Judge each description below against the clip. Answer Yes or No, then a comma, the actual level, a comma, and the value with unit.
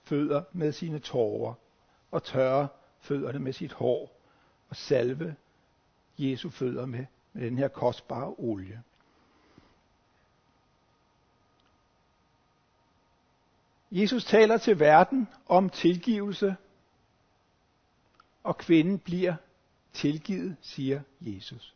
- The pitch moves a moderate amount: No, wide, 6.1 semitones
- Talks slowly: Yes, slow, 90 wpm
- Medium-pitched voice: Yes, medium, 150 Hz